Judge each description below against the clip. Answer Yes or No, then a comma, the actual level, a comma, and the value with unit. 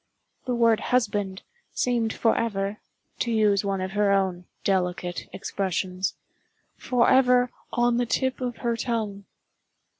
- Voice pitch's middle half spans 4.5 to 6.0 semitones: No, average, 3.7 semitones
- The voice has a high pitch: Yes, high, 215 Hz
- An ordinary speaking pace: No, slow, 110 wpm